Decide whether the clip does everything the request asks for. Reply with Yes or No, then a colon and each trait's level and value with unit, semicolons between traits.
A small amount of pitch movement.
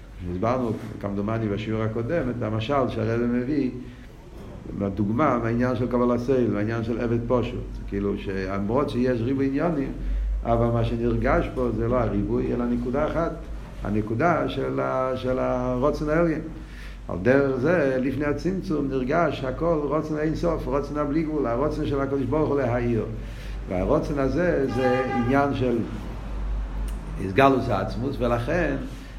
No: average, 3.8 semitones